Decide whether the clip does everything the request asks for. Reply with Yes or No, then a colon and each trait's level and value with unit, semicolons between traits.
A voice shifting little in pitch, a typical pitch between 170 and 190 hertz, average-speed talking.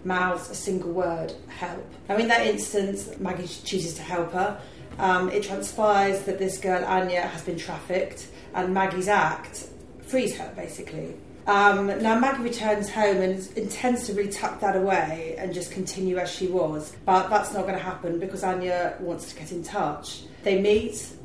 Yes: narrow, 2.2 semitones; medium, 185 Hz; average, 180 wpm